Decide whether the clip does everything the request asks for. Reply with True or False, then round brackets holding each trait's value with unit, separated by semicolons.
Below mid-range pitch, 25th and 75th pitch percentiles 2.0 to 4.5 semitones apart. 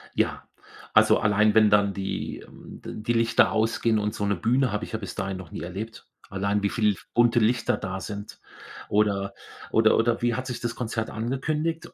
True (110 Hz; 2.5 semitones)